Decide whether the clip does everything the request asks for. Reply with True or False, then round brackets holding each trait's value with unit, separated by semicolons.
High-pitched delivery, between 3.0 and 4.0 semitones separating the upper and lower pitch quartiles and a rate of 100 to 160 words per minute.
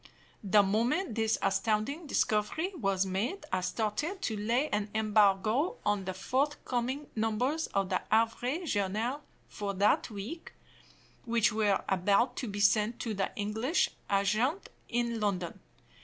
True (220 Hz; 3.7 semitones; 135 wpm)